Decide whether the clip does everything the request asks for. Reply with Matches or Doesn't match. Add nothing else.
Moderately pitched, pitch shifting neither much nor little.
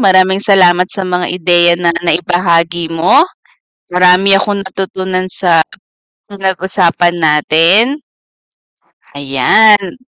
Doesn't match